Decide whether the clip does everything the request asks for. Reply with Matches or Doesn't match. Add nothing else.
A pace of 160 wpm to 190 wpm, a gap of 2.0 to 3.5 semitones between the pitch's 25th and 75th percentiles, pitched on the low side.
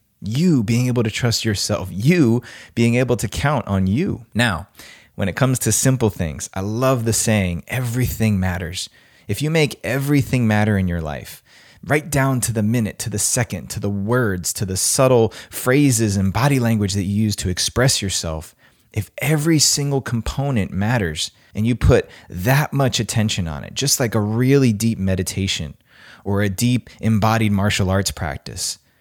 Doesn't match